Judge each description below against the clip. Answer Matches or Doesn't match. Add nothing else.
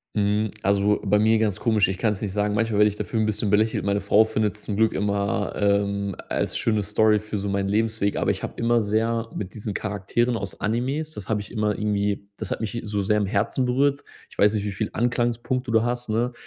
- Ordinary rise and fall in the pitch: Doesn't match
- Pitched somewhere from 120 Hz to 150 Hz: Doesn't match